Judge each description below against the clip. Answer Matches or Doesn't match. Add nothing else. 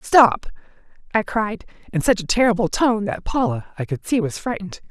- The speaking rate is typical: Matches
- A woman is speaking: Matches